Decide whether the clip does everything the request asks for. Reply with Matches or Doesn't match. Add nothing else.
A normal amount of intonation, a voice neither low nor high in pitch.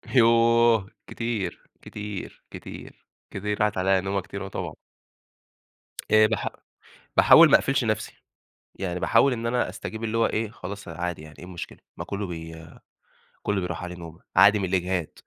Doesn't match